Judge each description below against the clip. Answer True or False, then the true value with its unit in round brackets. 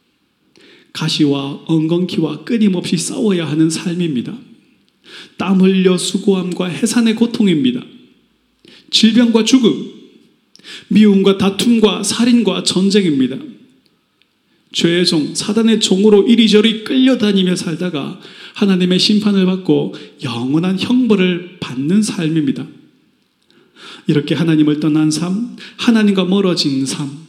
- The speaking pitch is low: False (195 Hz)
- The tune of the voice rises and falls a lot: False (4.8 semitones)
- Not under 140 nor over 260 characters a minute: True (250 characters per minute)